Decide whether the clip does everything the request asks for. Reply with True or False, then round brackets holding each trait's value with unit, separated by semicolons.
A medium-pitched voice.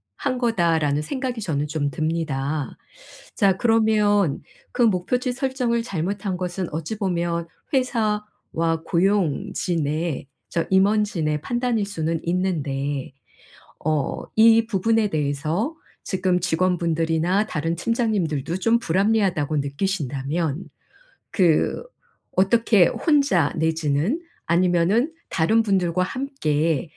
True (180 Hz)